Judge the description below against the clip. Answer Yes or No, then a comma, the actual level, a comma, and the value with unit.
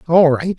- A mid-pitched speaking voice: Yes, medium, 165 Hz